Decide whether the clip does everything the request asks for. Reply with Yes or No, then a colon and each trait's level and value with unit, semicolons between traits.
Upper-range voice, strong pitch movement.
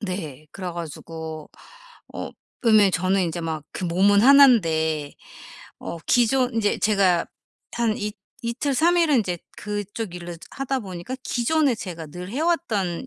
Yes: high, 200 Hz; wide, 5.9 semitones